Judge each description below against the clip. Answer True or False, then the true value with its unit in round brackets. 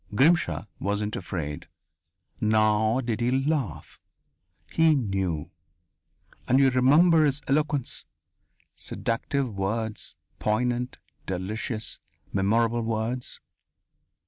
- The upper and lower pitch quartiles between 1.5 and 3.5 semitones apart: False (4.2 semitones)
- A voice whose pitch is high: False (115 Hz)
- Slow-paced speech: True (85 wpm)